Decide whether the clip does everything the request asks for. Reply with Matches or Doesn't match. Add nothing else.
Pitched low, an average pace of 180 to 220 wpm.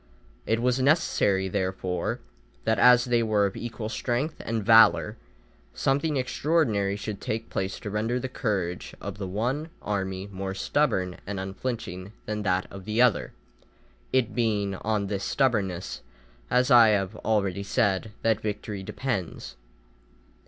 Doesn't match